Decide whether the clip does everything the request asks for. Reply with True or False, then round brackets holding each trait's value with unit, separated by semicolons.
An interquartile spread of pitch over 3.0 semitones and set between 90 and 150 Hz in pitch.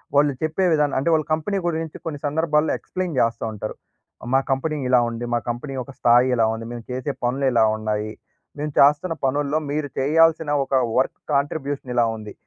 True (4.2 semitones; 140 Hz)